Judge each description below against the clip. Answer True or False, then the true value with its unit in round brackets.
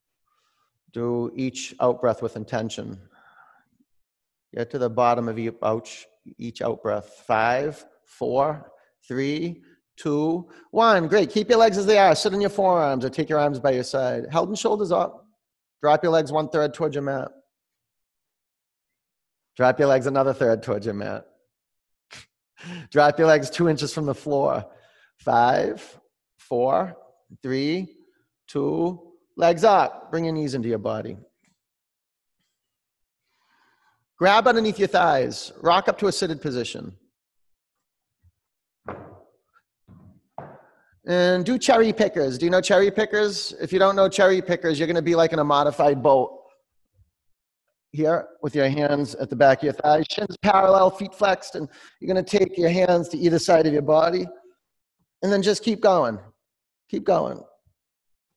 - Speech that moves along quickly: False (150 wpm)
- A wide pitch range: True (6.0 semitones)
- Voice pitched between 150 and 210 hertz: True (160 Hz)